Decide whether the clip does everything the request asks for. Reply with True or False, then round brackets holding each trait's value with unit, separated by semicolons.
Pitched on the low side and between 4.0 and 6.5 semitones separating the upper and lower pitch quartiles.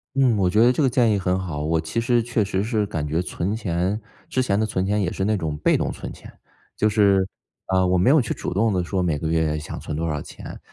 True (95 Hz; 4.5 semitones)